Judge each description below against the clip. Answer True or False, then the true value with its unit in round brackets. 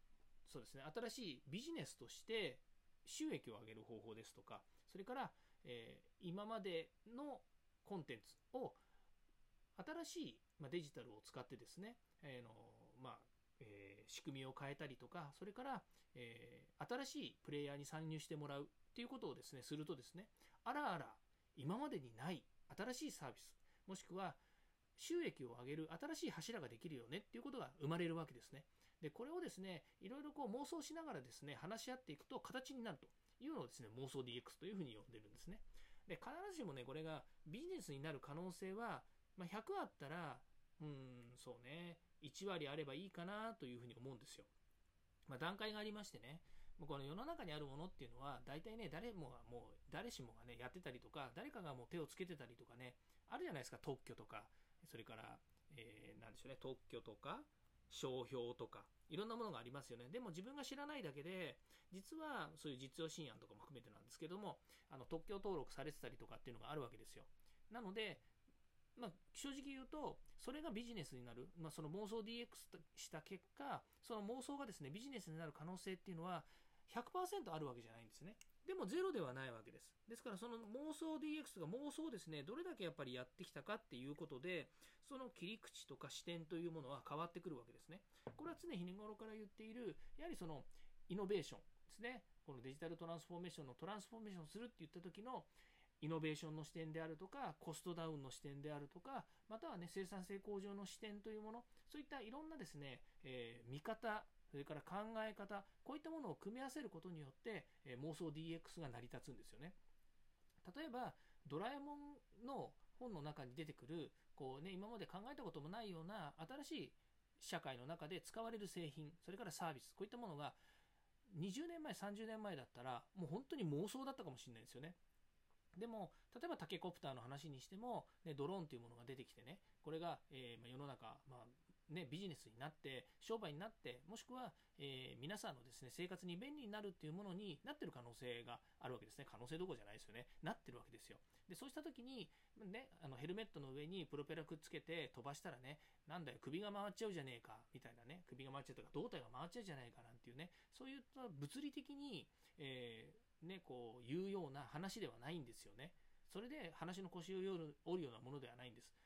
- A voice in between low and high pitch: True (165 Hz)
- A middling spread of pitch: False (7.8 semitones)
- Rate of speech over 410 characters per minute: True (420 characters per minute)